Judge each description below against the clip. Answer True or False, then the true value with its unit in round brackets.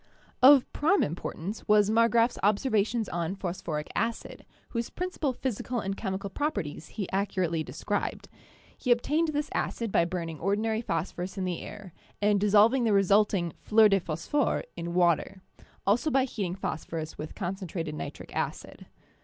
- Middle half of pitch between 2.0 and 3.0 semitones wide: False (4.8 semitones)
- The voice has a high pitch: True (200 Hz)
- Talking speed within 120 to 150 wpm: True (145 wpm)